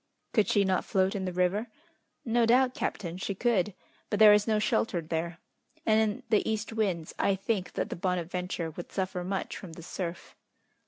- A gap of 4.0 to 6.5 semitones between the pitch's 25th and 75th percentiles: No, average, 3.3 semitones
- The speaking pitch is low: No, high, 190 Hz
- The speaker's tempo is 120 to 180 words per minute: No, average, 190 wpm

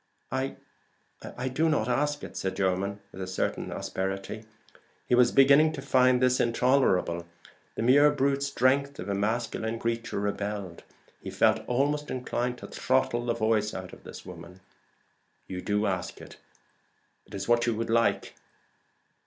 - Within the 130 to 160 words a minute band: Yes, average, 155 wpm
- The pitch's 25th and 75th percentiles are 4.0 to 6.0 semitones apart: Yes, average, 4.6 semitones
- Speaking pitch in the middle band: No, low, 115 Hz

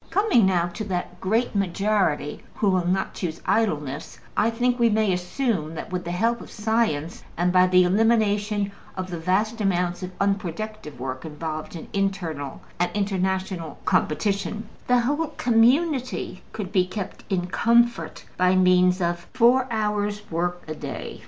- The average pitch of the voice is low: No, high, 190 Hz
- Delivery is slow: No, average, 155 wpm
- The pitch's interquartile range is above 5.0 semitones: No, average, 3.8 semitones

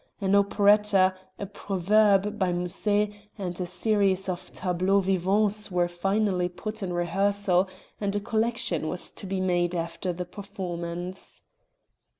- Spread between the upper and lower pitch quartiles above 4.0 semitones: No, narrow, 2.4 semitones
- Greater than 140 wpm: No, slow, 135 wpm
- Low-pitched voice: No, high, 190 Hz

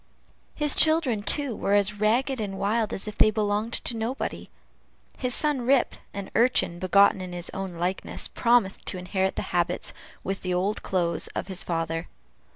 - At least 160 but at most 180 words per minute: Yes, average, 170 wpm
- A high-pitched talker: Yes, high, 205 Hz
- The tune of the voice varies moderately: Yes, average, 4.0 semitones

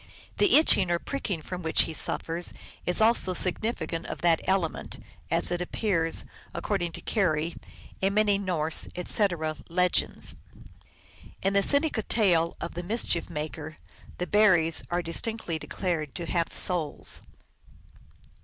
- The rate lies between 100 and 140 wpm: Yes, slow, 135 wpm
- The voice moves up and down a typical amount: Yes, average, 3.3 semitones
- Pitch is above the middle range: No, medium, 175 Hz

